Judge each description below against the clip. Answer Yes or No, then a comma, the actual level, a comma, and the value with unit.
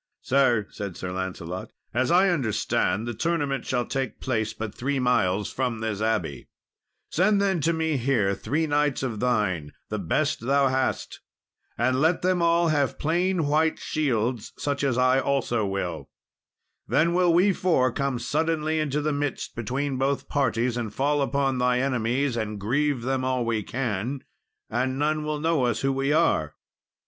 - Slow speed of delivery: No, average, 165 wpm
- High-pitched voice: No, low, 130 Hz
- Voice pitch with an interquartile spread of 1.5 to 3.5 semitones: No, average, 4.4 semitones